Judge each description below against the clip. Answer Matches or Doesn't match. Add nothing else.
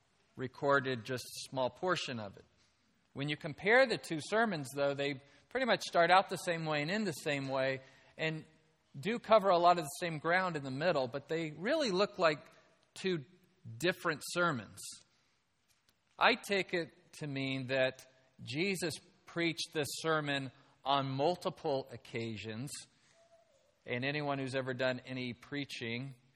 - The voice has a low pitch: Doesn't match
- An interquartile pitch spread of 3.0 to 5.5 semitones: Matches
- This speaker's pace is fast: Doesn't match